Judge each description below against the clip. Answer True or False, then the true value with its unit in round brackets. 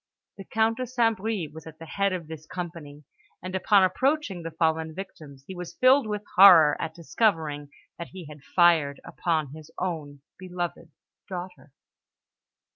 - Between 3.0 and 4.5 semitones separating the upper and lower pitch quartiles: True (3.7 semitones)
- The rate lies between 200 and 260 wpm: False (160 wpm)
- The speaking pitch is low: False (175 Hz)